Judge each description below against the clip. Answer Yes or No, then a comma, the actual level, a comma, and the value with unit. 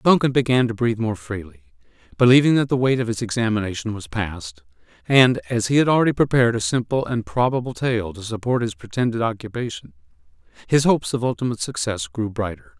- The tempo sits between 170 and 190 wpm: Yes, average, 180 wpm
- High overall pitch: No, low, 115 Hz